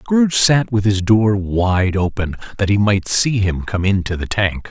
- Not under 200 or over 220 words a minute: Yes, fast, 205 wpm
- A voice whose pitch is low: Yes, low, 105 Hz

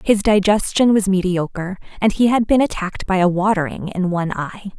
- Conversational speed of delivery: Yes, average, 190 wpm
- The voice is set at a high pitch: Yes, high, 195 Hz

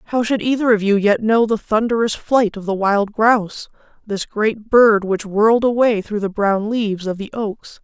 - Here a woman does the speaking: Yes, female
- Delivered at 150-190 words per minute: No, fast, 205 wpm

